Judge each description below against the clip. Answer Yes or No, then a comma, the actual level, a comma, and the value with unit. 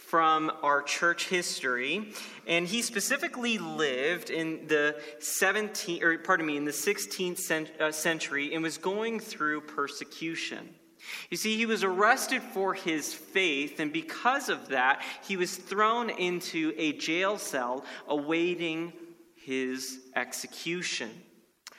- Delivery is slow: Yes, slow, 125 wpm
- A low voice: No, medium, 170 Hz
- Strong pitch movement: No, average, 4.3 semitones